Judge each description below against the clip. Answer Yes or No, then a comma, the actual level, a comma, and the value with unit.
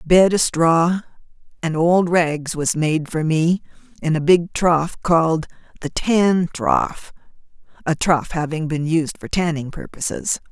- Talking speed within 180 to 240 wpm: No, average, 155 wpm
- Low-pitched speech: No, medium, 165 Hz